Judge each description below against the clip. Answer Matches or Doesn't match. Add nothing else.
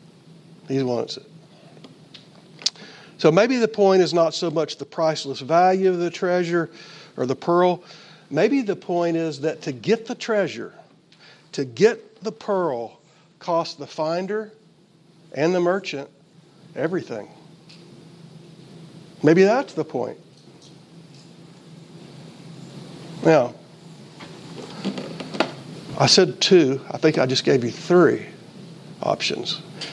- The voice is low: Doesn't match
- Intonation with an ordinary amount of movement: Doesn't match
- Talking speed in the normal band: Doesn't match